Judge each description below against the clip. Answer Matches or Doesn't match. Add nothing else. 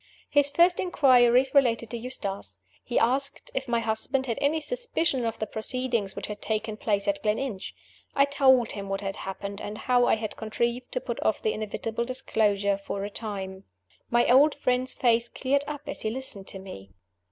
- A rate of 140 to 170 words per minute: Doesn't match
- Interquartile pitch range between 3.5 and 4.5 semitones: Matches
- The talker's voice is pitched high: Matches